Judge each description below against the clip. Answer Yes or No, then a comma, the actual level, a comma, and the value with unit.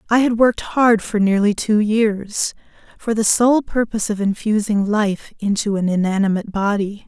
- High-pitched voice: Yes, high, 210 Hz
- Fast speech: No, average, 160 wpm